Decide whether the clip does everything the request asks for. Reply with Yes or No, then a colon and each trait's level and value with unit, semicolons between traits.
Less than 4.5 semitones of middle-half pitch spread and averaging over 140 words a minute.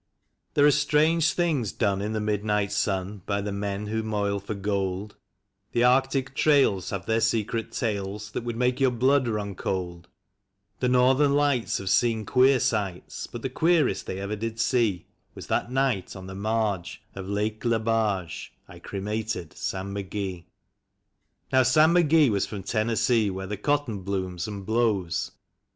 Yes: average, 4.1 semitones; average, 160 wpm